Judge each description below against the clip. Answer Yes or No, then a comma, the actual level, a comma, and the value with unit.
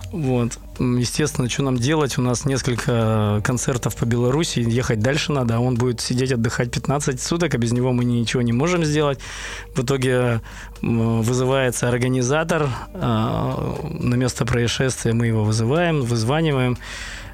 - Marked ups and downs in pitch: No, average, 2.7 semitones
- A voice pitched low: Yes, low, 125 Hz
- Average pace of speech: Yes, average, 140 wpm